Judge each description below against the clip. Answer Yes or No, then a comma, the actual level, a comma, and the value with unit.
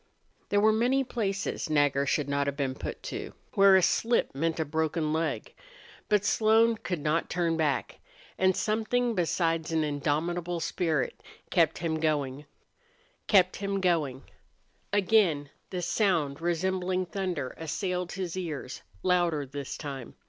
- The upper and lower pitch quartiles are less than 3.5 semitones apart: No, average, 4.3 semitones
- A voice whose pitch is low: No, medium, 170 Hz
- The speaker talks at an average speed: No, slow, 130 wpm